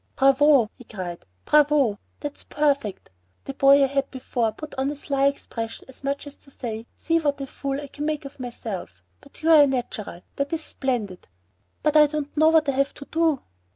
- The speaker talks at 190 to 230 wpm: Yes, average, 195 wpm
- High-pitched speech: Yes, very high, 275 Hz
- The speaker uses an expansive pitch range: No, average, 3.2 semitones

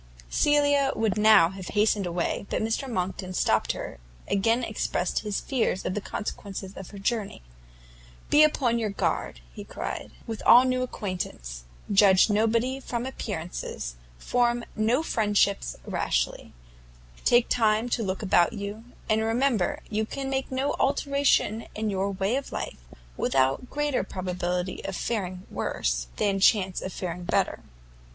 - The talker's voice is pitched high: Yes, high, 210 Hz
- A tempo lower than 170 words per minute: Yes, average, 145 wpm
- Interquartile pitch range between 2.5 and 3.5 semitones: No, average, 4.3 semitones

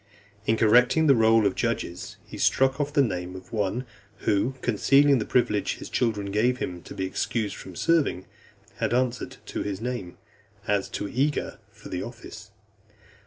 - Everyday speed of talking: Yes, average, 165 wpm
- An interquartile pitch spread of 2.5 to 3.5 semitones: No, average, 4.2 semitones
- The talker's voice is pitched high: No, low, 115 Hz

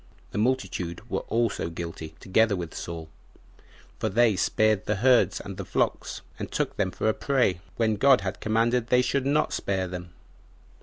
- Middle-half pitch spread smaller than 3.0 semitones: No, average, 4.6 semitones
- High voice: No, low, 105 Hz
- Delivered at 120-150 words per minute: No, average, 170 wpm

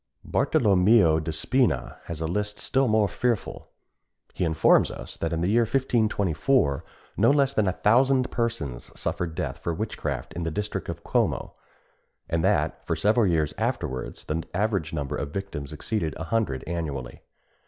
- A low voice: Yes, very low, 90 Hz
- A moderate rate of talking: Yes, average, 160 wpm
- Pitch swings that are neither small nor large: No, wide, 6.1 semitones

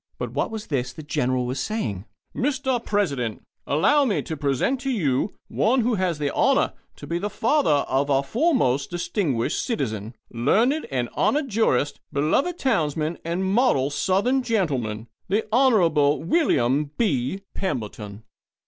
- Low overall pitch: No, medium, 170 Hz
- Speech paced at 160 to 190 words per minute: No, average, 145 wpm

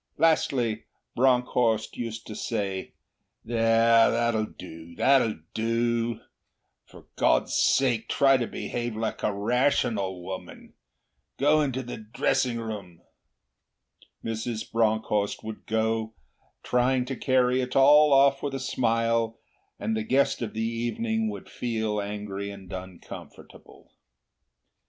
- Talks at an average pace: No, slow, 120 wpm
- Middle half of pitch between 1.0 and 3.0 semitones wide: Yes, narrow, 2.6 semitones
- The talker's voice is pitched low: Yes, low, 115 Hz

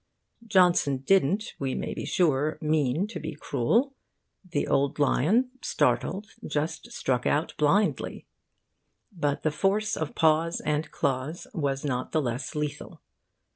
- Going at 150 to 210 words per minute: No, slow, 135 wpm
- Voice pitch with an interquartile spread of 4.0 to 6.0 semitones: Yes, average, 4.3 semitones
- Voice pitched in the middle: Yes, medium, 155 Hz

